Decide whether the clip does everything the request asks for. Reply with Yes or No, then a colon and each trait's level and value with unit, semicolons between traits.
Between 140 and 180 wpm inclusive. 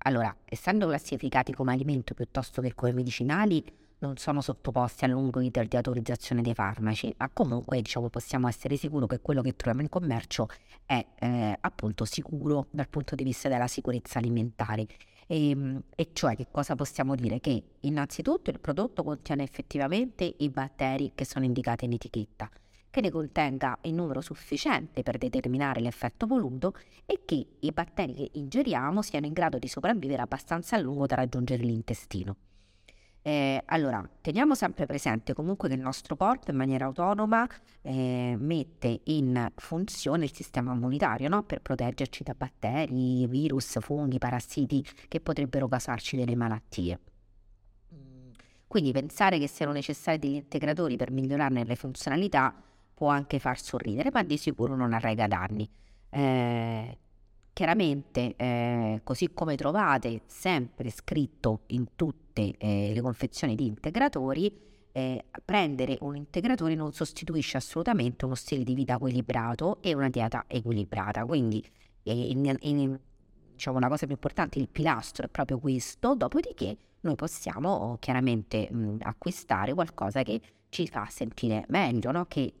Yes: average, 145 wpm